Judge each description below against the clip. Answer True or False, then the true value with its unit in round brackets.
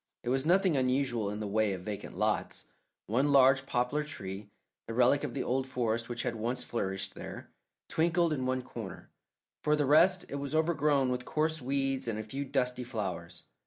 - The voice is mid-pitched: False (130 Hz)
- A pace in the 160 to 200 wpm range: True (190 wpm)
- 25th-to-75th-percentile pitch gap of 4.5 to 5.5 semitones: False (3.9 semitones)